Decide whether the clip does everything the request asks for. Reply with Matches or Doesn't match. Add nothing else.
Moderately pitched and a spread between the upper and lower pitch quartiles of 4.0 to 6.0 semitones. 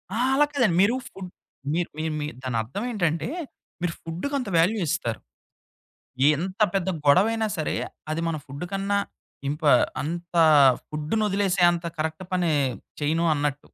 Matches